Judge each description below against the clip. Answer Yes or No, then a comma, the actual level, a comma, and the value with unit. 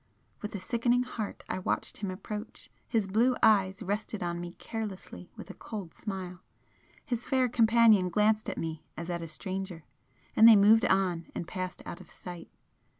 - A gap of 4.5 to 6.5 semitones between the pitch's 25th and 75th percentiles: No, average, 3.6 semitones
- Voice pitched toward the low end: No, high, 200 Hz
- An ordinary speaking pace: Yes, average, 175 wpm